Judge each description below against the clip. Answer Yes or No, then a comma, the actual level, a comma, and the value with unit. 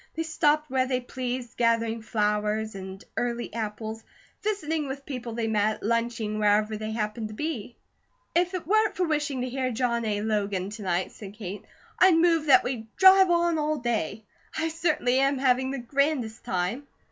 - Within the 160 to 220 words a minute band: Yes, average, 175 wpm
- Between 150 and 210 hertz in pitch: No, high, 240 Hz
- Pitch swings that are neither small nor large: No, wide, 5.7 semitones